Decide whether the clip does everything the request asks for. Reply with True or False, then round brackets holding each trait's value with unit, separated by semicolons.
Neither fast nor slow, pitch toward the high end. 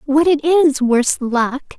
True (170 wpm; 285 Hz)